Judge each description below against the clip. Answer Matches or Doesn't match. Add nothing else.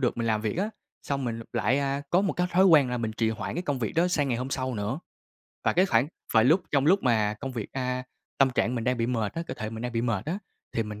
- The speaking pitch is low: Matches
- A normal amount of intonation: Matches